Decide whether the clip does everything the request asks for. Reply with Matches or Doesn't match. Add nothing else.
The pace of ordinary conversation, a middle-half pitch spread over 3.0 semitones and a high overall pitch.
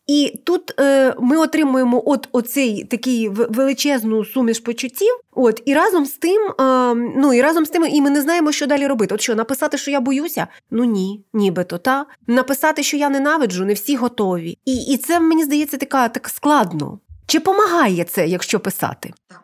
Doesn't match